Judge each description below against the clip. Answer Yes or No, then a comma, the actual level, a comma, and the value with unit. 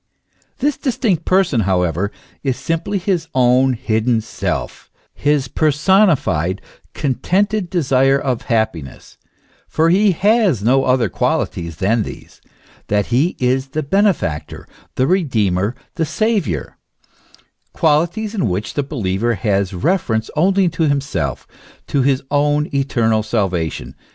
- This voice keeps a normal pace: No, slow, 120 wpm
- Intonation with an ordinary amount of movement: No, wide, 7.5 semitones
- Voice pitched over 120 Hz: Yes, low, 135 Hz